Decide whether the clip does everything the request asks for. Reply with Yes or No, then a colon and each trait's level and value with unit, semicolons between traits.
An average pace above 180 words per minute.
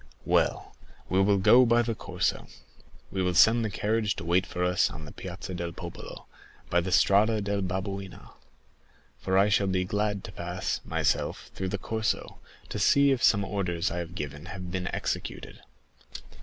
No: average, 175 wpm